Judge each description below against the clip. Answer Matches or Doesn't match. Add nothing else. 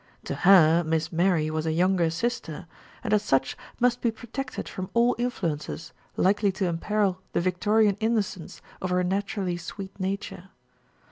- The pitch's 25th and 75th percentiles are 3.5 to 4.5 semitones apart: Matches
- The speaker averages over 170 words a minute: Doesn't match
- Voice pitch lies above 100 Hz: Matches